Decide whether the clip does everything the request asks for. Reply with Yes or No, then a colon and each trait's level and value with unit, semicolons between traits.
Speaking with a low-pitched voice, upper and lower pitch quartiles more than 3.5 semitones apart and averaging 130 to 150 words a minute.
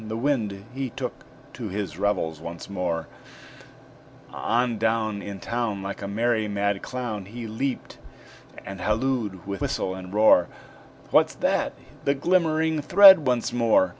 Yes: low, 110 Hz; average, 4.2 semitones; average, 140 wpm